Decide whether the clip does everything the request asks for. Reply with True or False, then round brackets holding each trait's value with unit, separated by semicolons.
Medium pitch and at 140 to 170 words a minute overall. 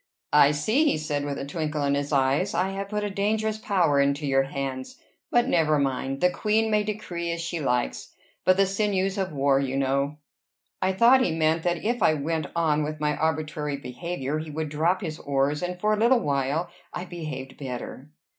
False (155 Hz; 200 wpm)